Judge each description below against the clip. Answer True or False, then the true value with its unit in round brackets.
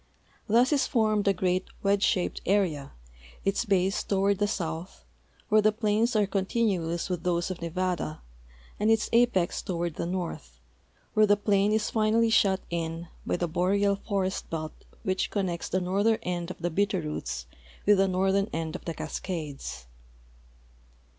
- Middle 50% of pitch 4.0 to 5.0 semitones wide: False (3.2 semitones)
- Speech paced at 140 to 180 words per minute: True (155 wpm)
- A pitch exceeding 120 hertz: True (190 Hz)